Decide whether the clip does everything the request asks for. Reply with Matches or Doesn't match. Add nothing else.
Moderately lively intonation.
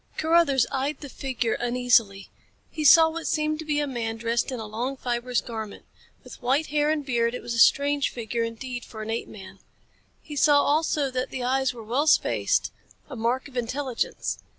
Matches